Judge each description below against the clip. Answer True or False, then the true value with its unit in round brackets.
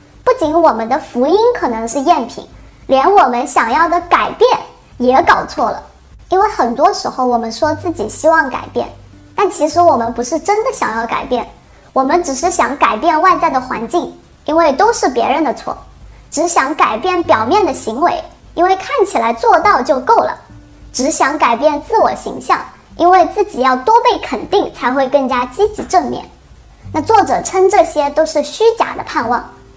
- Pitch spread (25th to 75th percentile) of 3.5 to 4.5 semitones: False (5.2 semitones)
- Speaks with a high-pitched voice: True (335 Hz)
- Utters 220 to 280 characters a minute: True (260 characters per minute)